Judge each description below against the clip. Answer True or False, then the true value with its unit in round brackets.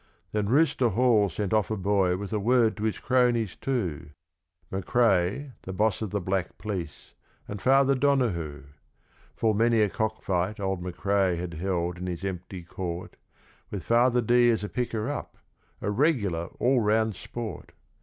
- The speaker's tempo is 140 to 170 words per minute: True (155 wpm)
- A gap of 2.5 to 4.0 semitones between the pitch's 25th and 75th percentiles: False (4.5 semitones)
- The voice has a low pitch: True (105 Hz)